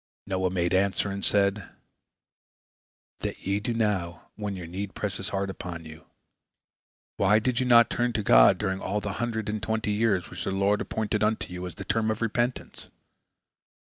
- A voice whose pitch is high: No, low, 100 Hz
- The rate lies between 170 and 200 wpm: Yes, average, 180 wpm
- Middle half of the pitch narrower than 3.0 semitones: Yes, narrow, 2.6 semitones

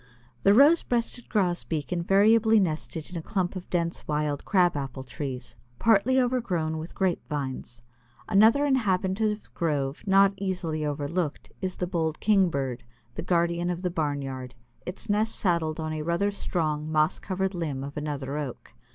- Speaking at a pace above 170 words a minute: No, average, 160 wpm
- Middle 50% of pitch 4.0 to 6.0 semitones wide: Yes, average, 4.6 semitones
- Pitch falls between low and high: Yes, medium, 170 Hz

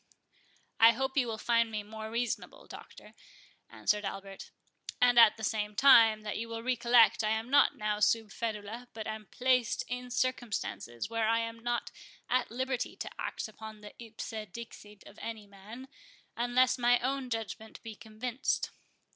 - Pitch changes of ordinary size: No, narrow, 2.2 semitones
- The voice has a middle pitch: No, high, 230 Hz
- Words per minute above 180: No, average, 165 wpm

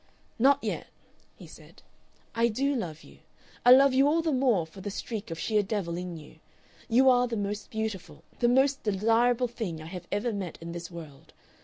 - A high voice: Yes, high, 215 Hz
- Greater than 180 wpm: Yes, average, 195 wpm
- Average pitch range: No, wide, 6.0 semitones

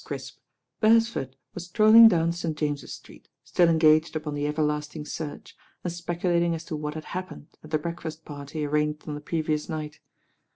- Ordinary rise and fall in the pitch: No, narrow, 2.3 semitones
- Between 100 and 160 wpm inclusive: No, average, 170 wpm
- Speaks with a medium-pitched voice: Yes, medium, 155 Hz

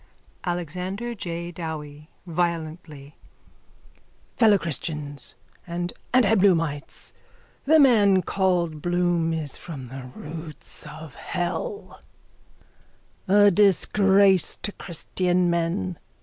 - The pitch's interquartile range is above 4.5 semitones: No, average, 3.5 semitones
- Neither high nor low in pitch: Yes, medium, 175 Hz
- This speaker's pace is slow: Yes, slow, 85 wpm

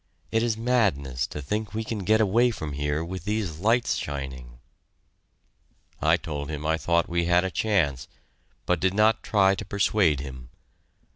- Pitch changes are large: Yes, wide, 6.6 semitones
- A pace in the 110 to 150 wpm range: No, average, 165 wpm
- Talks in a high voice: No, very low, 90 Hz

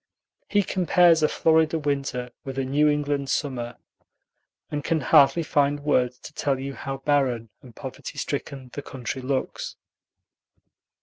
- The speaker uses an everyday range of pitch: No, narrow, 2.3 semitones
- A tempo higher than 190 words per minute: No, average, 140 wpm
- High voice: No, medium, 140 Hz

